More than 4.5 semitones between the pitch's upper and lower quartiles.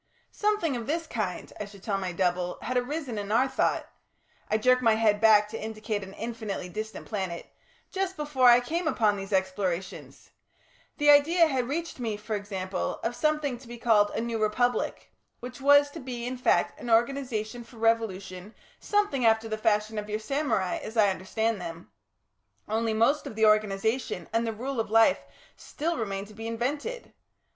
No: average, 3.6 semitones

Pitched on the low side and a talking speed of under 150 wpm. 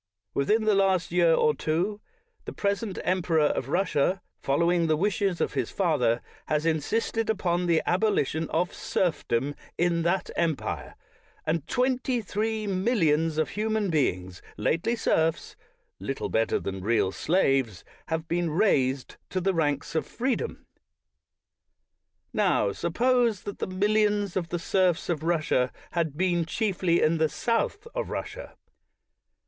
No: medium, 170 Hz; average, 140 wpm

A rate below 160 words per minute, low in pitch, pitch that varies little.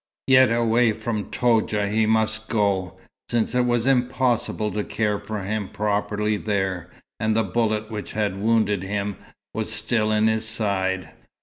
Yes: average, 150 wpm; low, 110 Hz; narrow, 1.8 semitones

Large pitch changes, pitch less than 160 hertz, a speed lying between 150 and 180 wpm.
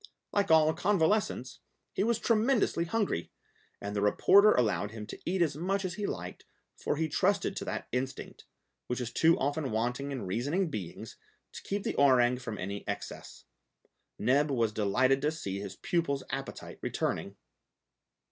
Yes: wide, 7.5 semitones; medium, 140 Hz; average, 160 wpm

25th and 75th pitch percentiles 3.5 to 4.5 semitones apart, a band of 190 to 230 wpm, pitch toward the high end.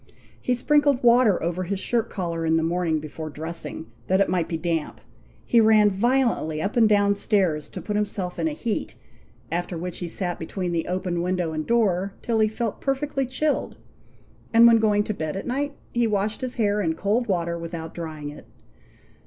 No: wide, 5.4 semitones; average, 195 wpm; high, 195 Hz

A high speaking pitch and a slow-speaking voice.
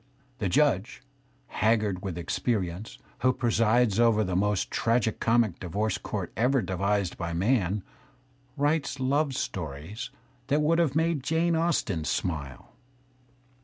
No: low, 110 Hz; slow, 125 wpm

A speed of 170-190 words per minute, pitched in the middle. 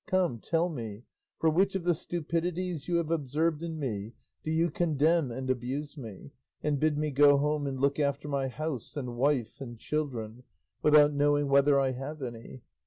Yes: average, 180 wpm; medium, 145 Hz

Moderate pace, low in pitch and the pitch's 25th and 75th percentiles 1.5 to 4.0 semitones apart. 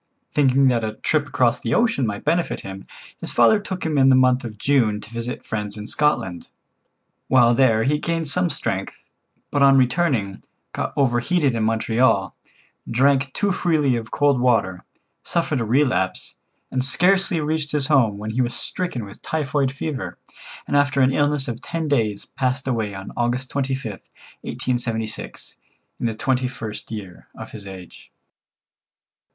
No: average, 160 wpm; low, 130 Hz; average, 4.5 semitones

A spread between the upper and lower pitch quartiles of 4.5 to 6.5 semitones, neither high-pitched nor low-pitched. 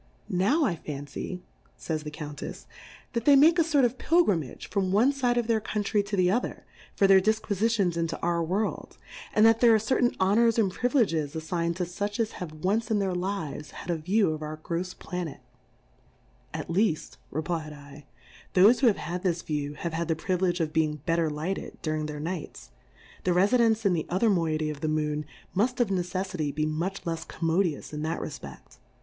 Yes: average, 5.2 semitones; medium, 180 Hz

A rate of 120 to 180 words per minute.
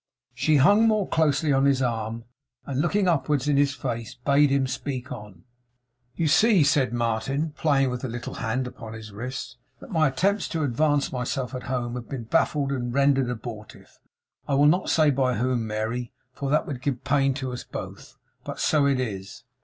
No: average, 190 wpm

